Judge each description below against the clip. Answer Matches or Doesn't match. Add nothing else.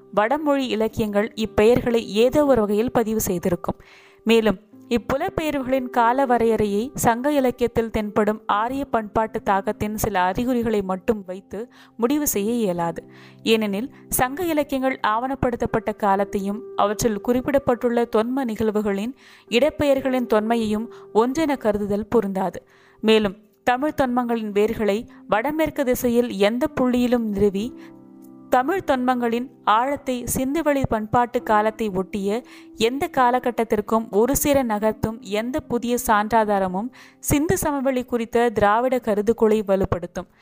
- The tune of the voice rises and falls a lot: Doesn't match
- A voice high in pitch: Matches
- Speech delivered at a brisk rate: Doesn't match